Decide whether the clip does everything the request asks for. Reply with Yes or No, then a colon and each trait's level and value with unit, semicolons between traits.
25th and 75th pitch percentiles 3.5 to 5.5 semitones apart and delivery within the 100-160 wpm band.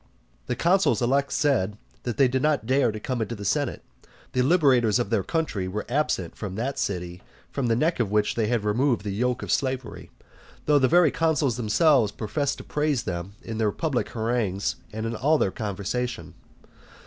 No: average, 4.9 semitones; average, 190 wpm